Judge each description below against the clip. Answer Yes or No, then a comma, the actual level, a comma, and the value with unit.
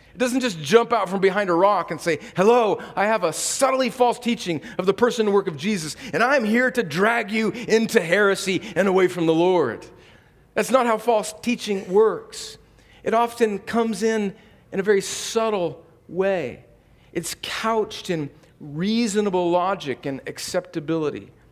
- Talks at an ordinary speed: Yes, average, 165 wpm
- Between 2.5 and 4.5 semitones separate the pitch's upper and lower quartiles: No, average, 4.9 semitones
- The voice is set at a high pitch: Yes, high, 205 Hz